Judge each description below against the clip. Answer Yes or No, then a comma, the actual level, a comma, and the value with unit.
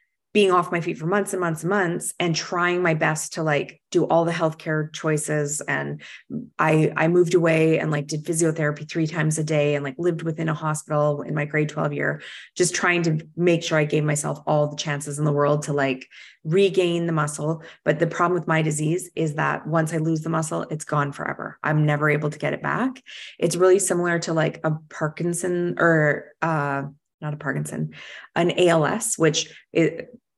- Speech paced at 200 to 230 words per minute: Yes, fast, 205 wpm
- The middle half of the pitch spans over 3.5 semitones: No, narrow, 2.5 semitones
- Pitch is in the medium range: Yes, medium, 160 Hz